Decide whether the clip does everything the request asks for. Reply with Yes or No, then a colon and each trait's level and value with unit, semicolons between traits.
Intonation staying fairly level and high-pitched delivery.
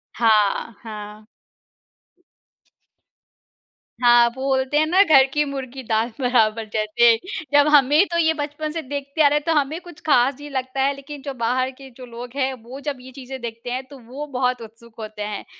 No: average, 3.5 semitones; very high, 260 Hz